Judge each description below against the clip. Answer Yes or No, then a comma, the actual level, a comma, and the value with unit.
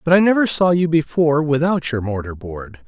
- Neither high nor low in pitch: Yes, medium, 150 Hz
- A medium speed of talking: No, fast, 210 wpm